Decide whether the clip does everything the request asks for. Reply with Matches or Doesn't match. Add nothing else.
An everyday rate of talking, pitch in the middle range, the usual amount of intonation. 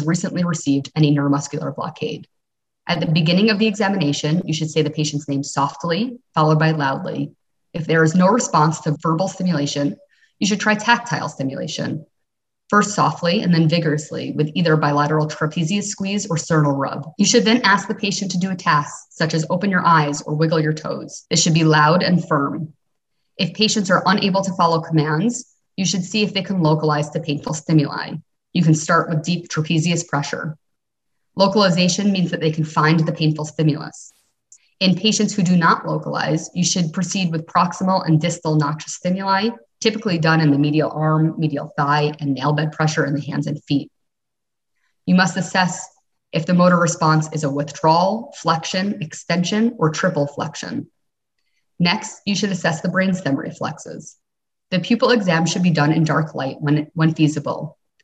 Matches